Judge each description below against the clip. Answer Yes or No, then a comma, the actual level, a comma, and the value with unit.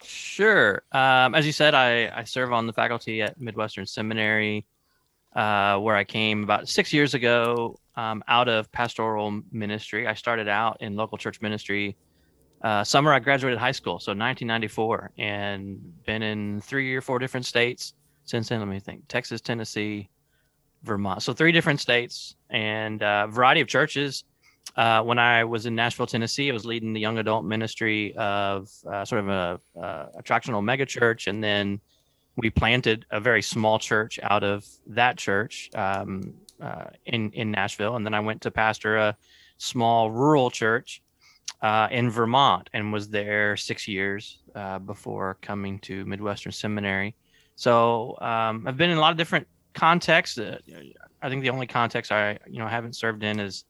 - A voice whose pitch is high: No, low, 110 Hz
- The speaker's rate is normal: Yes, average, 170 wpm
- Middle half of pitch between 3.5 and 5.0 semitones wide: No, average, 2.8 semitones